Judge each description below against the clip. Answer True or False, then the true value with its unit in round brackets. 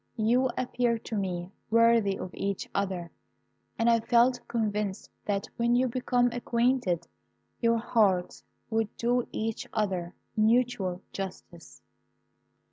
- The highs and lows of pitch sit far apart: False (3.5 semitones)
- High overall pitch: True (225 Hz)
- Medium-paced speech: False (120 wpm)